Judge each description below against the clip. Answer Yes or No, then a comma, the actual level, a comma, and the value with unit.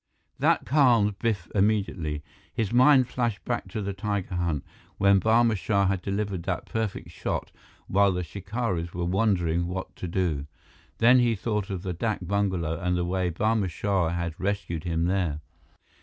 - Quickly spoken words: No, average, 165 wpm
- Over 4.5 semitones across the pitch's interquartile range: No, average, 3.6 semitones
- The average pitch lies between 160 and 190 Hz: No, very low, 95 Hz